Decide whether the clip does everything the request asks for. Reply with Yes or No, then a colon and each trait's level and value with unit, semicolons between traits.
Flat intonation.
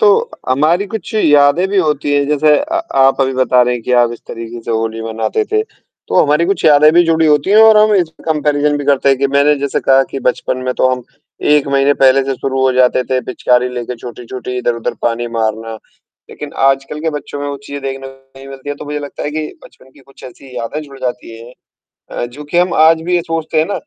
No: average, 3.3 semitones